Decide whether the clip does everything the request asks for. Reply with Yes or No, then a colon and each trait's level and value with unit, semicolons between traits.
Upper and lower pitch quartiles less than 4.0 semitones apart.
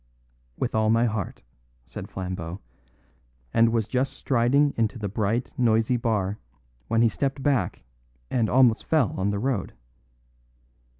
Yes: average, 3.5 semitones